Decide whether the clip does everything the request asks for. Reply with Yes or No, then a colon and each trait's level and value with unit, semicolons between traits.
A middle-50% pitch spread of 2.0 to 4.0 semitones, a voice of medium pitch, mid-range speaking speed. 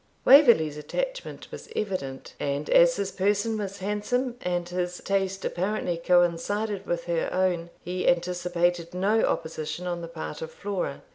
Yes: average, 3.1 semitones; medium, 180 Hz; average, 145 wpm